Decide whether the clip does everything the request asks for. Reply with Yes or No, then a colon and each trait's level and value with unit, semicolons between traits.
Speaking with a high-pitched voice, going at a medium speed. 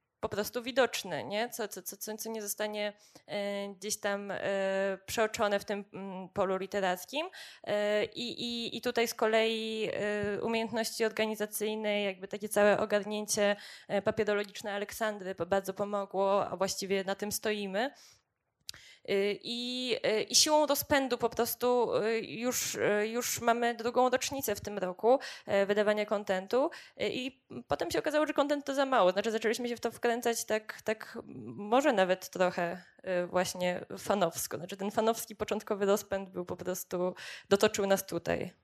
Yes: high, 210 Hz; average, 135 wpm